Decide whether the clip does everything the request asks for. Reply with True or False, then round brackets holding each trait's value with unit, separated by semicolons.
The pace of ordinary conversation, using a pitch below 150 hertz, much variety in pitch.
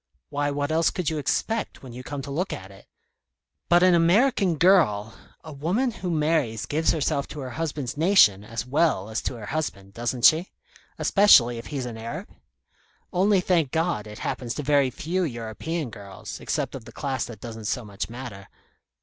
True (190 wpm; 140 Hz; 6.3 semitones)